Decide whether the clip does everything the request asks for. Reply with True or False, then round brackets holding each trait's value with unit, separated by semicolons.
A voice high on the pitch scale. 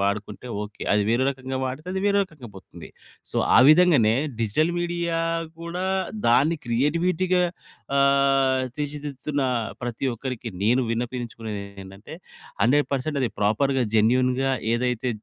False (130 Hz)